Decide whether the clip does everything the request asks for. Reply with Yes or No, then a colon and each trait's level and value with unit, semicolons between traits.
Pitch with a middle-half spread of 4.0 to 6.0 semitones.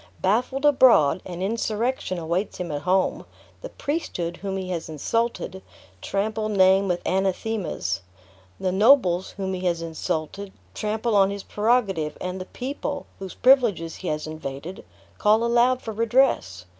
Yes: average, 4.6 semitones